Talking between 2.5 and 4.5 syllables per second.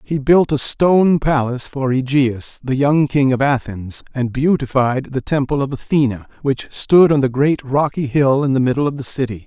No: 4.9 syllables/s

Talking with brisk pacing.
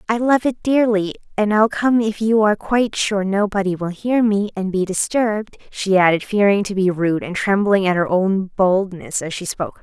Yes: fast, 210 wpm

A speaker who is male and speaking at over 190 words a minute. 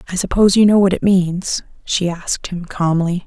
No: female; average, 200 wpm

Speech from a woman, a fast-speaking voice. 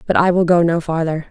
Yes: female; fast, 275 wpm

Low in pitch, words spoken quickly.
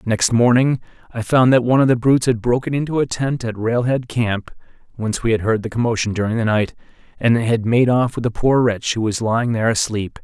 Yes: low, 115 Hz; fast, 215 wpm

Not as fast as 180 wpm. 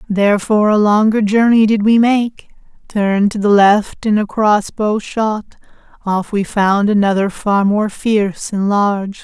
Yes: average, 155 wpm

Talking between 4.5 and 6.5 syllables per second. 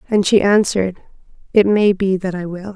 Yes: 5.3 syllables/s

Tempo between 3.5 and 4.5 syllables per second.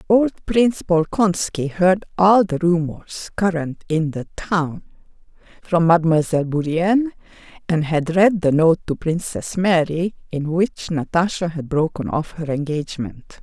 Yes: 4.3 syllables/s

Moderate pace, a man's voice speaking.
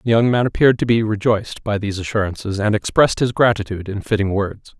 No: fast, 215 wpm; male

